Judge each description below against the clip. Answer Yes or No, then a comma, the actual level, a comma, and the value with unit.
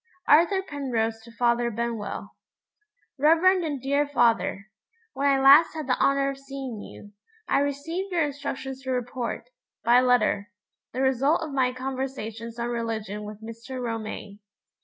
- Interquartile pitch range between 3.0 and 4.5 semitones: Yes, average, 3.4 semitones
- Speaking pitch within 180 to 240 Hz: No, very high, 255 Hz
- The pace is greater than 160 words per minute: No, average, 145 wpm